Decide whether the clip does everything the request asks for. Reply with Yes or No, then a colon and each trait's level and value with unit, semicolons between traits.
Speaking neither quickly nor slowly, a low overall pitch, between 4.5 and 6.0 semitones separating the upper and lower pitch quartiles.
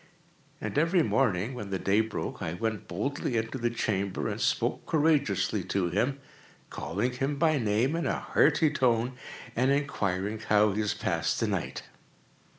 Yes: average, 160 wpm; low, 115 Hz; wide, 5.4 semitones